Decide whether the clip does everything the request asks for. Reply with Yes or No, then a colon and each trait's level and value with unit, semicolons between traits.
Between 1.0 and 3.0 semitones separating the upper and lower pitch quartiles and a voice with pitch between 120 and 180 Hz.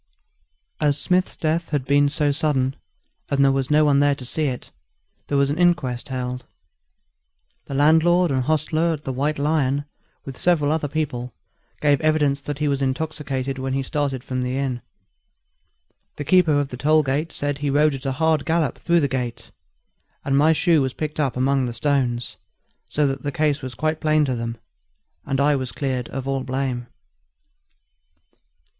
Yes: narrow, 2.6 semitones; medium, 140 Hz